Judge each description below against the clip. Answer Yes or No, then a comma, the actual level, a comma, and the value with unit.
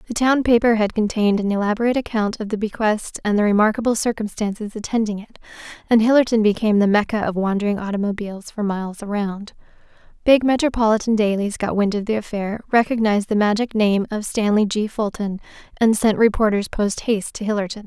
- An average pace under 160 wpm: No, average, 170 wpm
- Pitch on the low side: No, high, 215 Hz